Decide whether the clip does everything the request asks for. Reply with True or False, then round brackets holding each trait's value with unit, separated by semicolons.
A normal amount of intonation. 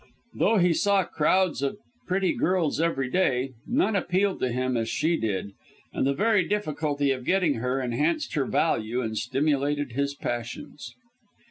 False (6.2 semitones)